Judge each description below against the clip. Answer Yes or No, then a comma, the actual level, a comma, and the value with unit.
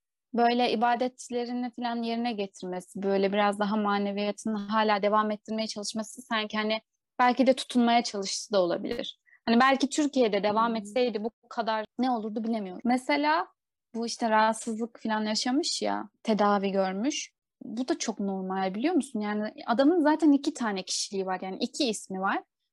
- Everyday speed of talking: No, fast, 150 wpm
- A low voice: No, high, 225 Hz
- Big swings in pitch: No, average, 3.2 semitones